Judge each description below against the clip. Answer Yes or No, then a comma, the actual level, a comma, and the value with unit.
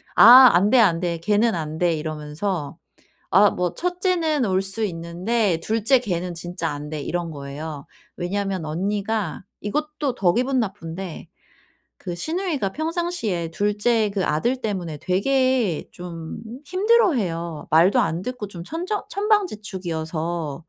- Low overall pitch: No, high, 195 Hz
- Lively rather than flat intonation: Yes, wide, 6.9 semitones